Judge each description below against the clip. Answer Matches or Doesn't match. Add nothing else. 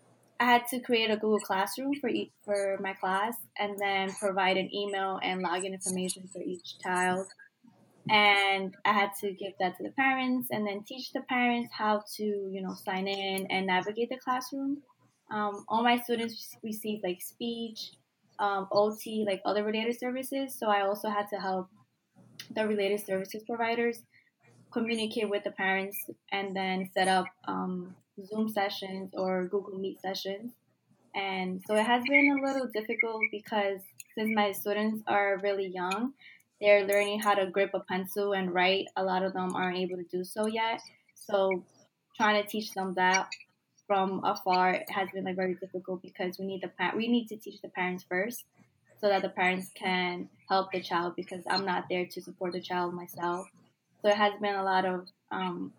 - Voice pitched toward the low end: Doesn't match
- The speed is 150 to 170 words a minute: Doesn't match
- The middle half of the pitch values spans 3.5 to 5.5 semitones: Doesn't match